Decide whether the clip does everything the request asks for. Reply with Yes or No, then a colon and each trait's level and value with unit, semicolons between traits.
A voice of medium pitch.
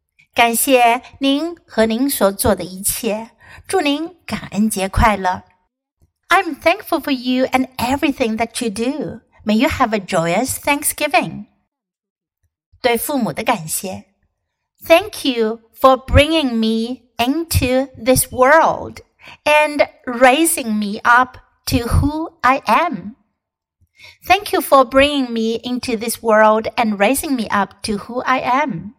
No: high, 245 Hz